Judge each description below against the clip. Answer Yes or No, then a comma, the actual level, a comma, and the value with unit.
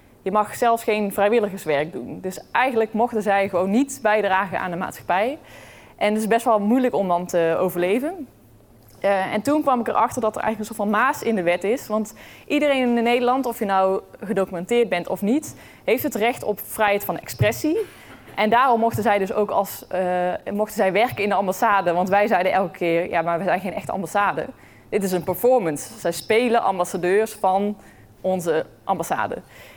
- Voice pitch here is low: No, high, 205 Hz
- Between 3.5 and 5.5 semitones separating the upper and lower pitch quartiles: Yes, average, 3.8 semitones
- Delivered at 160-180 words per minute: No, average, 195 wpm